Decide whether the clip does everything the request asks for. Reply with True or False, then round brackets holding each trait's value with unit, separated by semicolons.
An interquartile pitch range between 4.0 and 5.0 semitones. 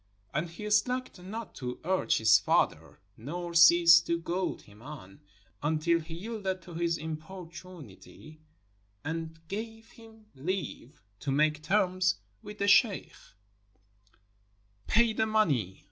True (4.5 semitones)